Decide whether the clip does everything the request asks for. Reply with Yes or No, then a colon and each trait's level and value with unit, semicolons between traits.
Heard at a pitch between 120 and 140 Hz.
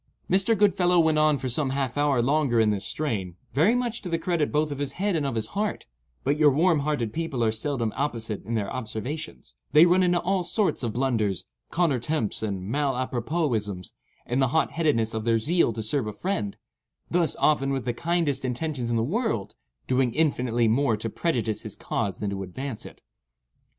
Yes: low, 135 Hz